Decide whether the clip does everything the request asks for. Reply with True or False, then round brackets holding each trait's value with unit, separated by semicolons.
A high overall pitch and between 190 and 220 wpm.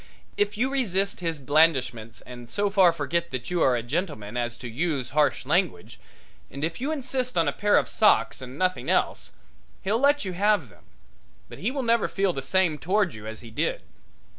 False (170 Hz; 200 wpm)